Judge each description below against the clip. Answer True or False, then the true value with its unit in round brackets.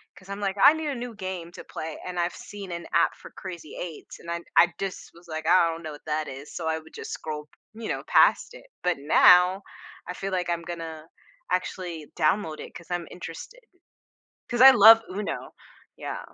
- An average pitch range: True (3.4 semitones)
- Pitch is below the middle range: False (175 Hz)